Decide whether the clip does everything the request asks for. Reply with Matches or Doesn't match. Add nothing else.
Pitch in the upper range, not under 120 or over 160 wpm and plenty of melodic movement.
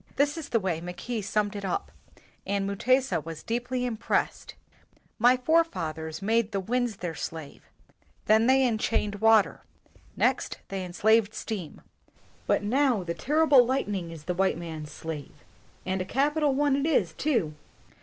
Matches